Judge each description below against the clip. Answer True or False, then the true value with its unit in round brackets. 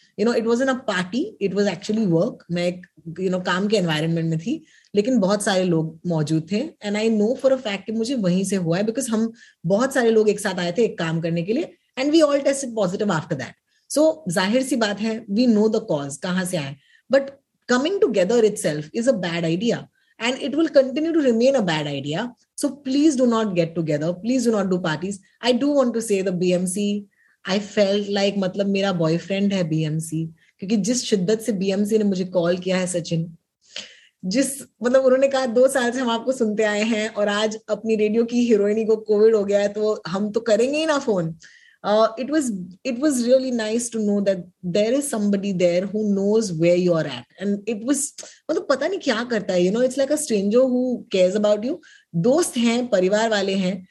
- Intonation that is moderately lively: True (5.0 semitones)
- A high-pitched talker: True (210 Hz)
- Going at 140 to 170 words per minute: False (180 wpm)